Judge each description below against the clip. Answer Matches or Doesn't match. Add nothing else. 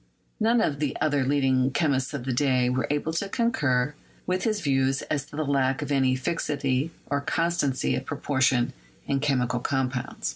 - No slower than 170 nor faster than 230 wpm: Matches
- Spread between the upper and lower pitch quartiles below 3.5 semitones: Matches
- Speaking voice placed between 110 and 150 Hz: Matches